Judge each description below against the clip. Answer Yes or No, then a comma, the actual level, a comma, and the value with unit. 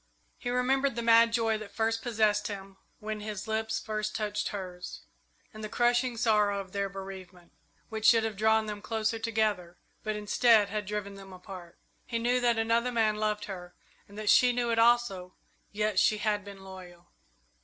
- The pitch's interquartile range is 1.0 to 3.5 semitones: Yes, narrow, 2.4 semitones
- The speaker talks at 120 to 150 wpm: No, average, 175 wpm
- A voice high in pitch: Yes, high, 215 Hz